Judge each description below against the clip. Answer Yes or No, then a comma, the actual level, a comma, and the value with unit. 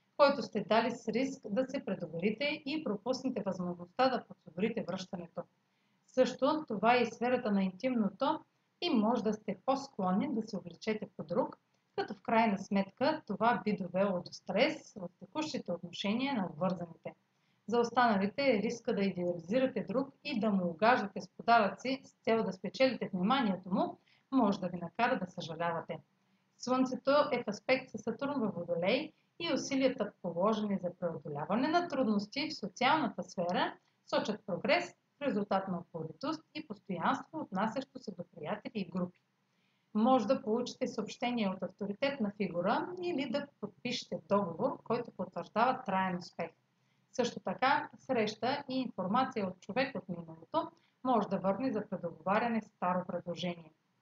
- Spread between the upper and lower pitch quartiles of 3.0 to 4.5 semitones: No, wide, 5.6 semitones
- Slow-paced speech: No, average, 150 wpm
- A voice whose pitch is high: Yes, high, 220 Hz